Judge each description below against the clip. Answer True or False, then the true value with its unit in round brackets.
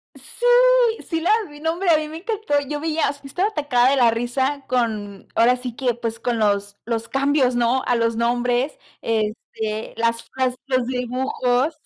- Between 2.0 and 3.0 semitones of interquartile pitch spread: False (3.9 semitones)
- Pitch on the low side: False (250 Hz)